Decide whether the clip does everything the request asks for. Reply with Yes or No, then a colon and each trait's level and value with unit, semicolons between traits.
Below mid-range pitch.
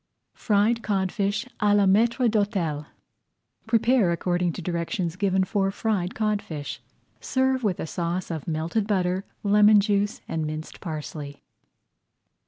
No: high, 195 Hz